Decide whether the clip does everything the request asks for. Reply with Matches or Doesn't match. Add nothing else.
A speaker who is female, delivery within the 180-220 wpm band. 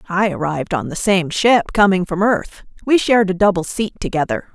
Matches